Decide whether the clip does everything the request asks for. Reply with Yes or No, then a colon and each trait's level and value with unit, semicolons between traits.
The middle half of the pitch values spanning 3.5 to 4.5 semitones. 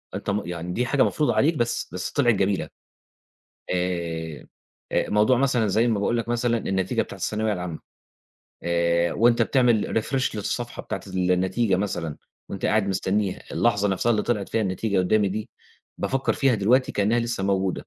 Yes: average, 4.2 semitones